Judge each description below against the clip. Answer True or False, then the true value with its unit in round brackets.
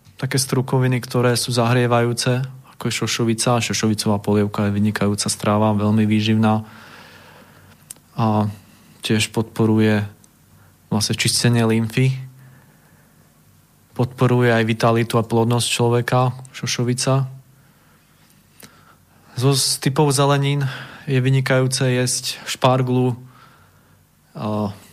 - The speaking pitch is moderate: False (120 Hz)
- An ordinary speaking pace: False (90 wpm)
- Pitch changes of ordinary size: True (3.3 semitones)